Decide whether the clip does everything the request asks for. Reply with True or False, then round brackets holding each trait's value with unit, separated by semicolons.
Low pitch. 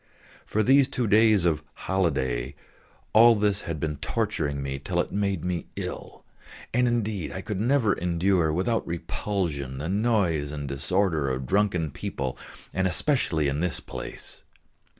True (90 Hz)